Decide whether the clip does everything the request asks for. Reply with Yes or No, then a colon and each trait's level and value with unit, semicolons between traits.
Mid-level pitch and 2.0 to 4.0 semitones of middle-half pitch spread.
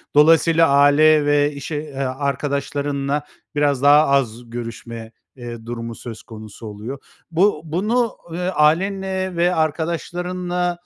No: medium, 145 Hz; average, 4.8 semitones